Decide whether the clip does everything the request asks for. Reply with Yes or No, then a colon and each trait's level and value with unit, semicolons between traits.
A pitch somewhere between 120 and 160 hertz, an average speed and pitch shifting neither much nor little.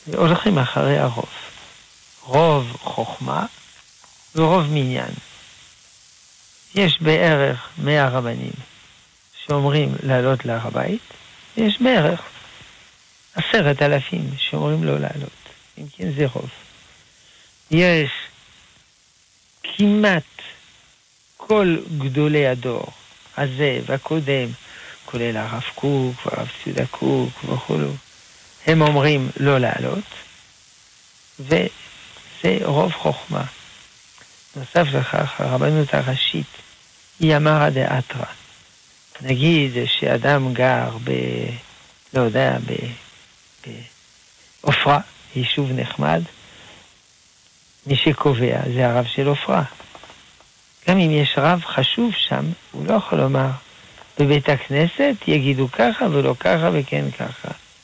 No: medium, 140 Hz; slow, 90 wpm; average, 3.9 semitones